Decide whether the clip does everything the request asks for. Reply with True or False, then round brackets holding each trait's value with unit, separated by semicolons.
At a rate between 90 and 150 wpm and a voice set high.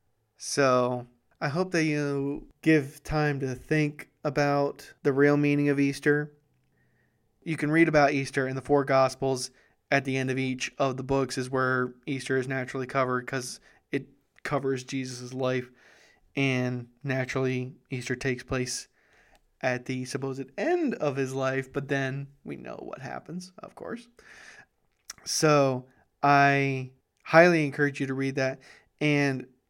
False (145 wpm; 135 Hz)